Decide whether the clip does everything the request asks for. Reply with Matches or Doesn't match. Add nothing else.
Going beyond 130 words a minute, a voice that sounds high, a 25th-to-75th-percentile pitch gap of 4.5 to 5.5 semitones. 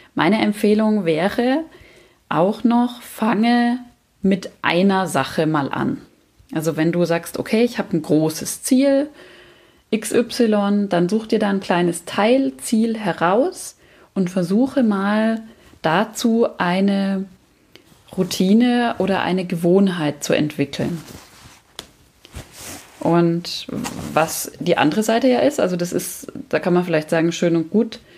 Doesn't match